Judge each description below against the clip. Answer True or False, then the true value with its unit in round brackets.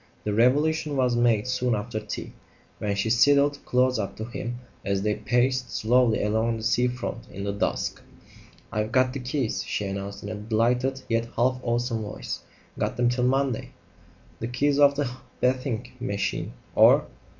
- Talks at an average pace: True (170 wpm)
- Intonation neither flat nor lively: True (3.0 semitones)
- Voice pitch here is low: True (120 Hz)